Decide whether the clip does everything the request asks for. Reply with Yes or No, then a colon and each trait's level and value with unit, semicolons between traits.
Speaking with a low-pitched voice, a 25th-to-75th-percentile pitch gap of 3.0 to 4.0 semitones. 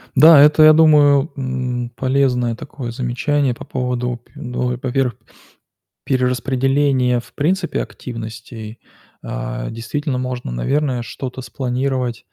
No: low, 125 Hz; narrow, 2.4 semitones